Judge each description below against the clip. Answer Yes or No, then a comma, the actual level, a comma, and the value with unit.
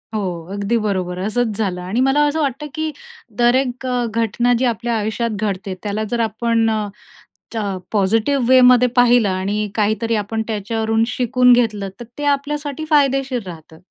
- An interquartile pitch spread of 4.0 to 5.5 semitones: No, average, 3.3 semitones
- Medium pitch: No, high, 230 Hz